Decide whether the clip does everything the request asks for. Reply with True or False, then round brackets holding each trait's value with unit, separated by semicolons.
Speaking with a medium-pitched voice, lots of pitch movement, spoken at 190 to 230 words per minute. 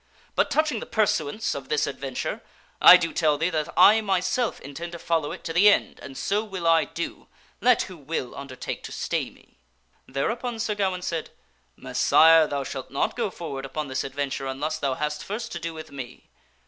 True (165 Hz; 6.1 semitones; 200 wpm)